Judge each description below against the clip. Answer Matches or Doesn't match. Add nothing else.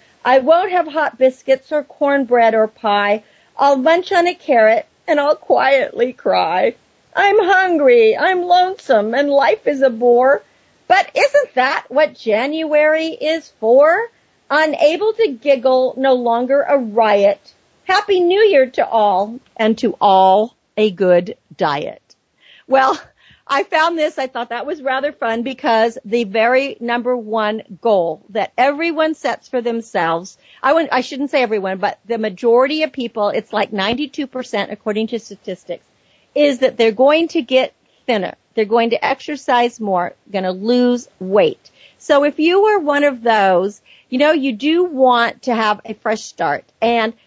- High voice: Matches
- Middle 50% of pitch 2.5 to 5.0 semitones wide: Doesn't match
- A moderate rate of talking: Matches